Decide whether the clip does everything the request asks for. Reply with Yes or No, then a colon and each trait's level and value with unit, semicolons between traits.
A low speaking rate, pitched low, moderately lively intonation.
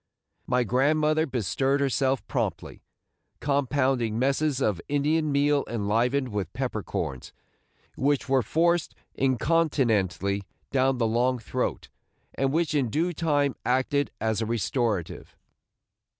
Yes: slow, 115 wpm; low, 130 Hz; average, 3.9 semitones